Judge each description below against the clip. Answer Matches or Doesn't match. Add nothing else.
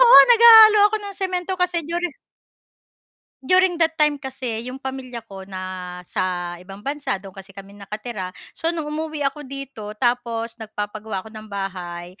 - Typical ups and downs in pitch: Doesn't match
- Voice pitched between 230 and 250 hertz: Matches